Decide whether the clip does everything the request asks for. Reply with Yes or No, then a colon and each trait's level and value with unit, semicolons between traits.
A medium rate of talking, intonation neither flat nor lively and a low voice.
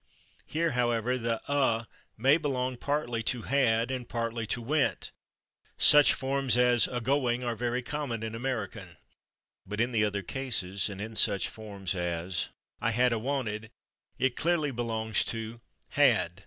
Yes: average, 155 wpm; average, 3.2 semitones; low, 120 Hz